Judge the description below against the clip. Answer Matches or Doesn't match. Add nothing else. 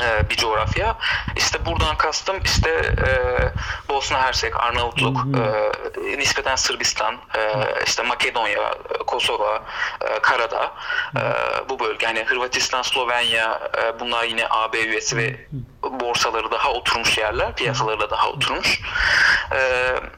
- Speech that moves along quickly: Doesn't match